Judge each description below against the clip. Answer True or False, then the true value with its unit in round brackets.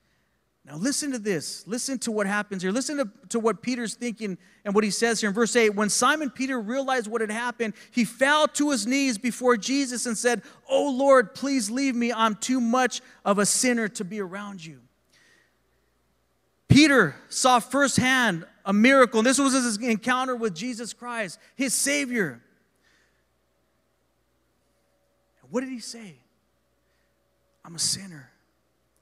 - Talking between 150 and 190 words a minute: True (160 wpm)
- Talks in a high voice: True (230 Hz)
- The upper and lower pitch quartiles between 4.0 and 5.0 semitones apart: True (4.3 semitones)